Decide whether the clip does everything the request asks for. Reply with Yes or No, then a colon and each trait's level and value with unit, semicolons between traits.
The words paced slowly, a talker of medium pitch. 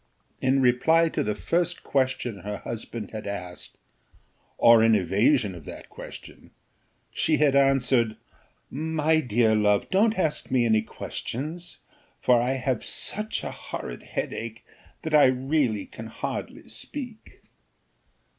No: slow, 130 wpm; low, 125 Hz